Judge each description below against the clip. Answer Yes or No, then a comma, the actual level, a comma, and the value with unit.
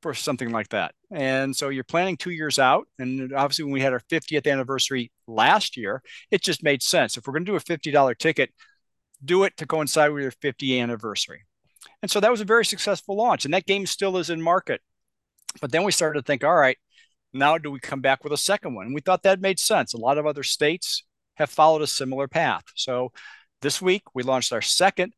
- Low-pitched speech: No, medium, 150 Hz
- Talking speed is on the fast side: Yes, fast, 230 wpm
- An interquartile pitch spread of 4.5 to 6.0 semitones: Yes, average, 5.2 semitones